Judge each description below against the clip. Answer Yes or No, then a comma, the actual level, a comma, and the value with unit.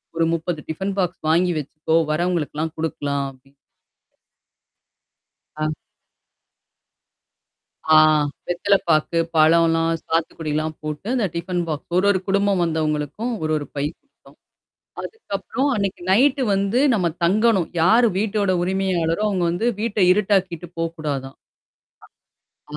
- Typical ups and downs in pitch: Yes, average, 4.1 semitones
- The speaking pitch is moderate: Yes, medium, 175 Hz